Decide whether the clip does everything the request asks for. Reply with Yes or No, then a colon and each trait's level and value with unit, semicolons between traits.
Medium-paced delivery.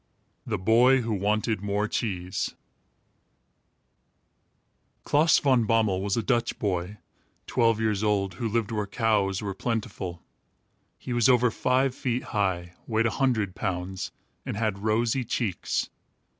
No: slow, 130 wpm